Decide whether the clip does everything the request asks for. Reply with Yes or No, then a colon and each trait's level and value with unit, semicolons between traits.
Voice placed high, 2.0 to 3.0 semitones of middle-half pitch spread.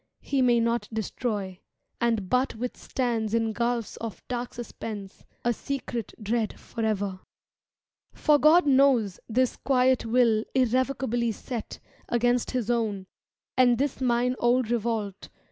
Yes: high, 235 Hz; narrow, 2.4 semitones